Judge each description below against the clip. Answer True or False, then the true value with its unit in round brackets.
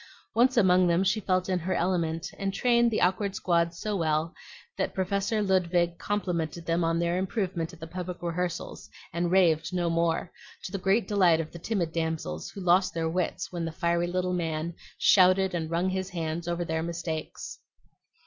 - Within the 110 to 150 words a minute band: False (185 wpm)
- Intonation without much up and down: True (2.2 semitones)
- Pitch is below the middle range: False (175 Hz)